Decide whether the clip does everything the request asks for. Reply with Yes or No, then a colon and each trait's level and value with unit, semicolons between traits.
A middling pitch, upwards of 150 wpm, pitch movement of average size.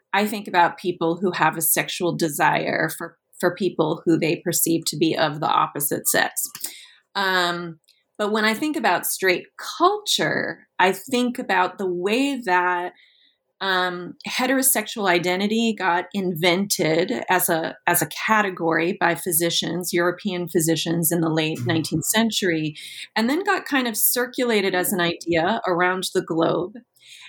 No: medium, 180 Hz; average, 145 wpm; average, 3.7 semitones